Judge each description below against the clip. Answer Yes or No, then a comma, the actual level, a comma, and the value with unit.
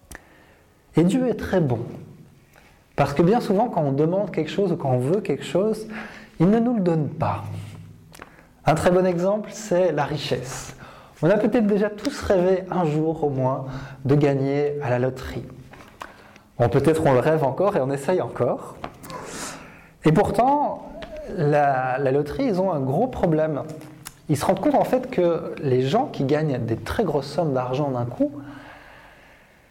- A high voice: No, medium, 155 Hz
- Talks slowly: No, average, 175 wpm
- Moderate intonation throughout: No, wide, 5.7 semitones